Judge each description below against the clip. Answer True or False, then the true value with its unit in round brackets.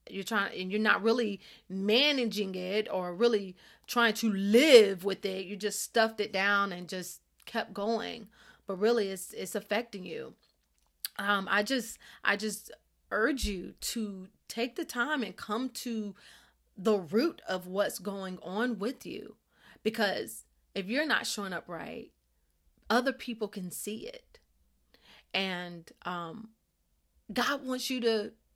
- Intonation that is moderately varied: True (3.3 semitones)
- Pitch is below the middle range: False (210 Hz)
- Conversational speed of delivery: True (145 wpm)